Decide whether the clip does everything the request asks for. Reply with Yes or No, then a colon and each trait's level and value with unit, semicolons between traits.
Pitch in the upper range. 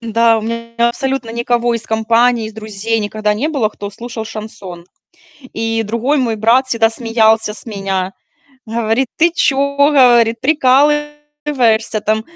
Yes: high, 230 Hz